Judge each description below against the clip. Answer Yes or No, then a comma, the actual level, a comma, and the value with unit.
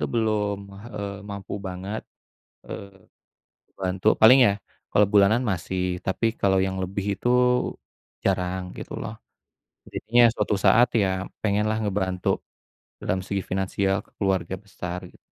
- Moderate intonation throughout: No, narrow, 1.8 semitones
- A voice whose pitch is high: No, low, 100 Hz